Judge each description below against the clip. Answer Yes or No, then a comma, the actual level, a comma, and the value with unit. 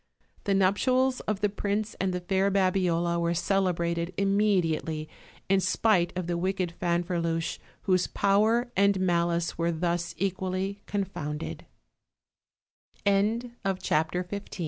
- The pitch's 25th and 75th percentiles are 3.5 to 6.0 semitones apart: No, narrow, 2.6 semitones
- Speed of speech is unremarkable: No, slow, 110 wpm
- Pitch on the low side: No, medium, 185 Hz